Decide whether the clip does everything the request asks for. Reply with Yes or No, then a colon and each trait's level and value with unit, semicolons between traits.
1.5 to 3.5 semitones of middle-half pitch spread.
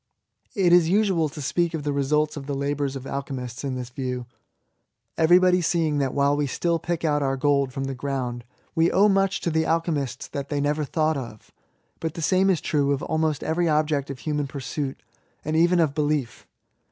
Yes: average, 3.1 semitones